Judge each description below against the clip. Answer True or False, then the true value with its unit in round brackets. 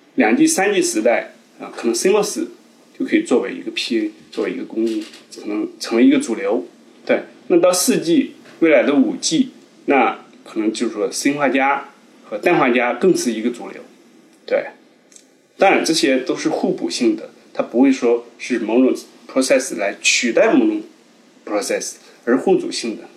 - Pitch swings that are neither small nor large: True (3.0 semitones)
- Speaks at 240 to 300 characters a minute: True (275 characters per minute)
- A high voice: True (320 Hz)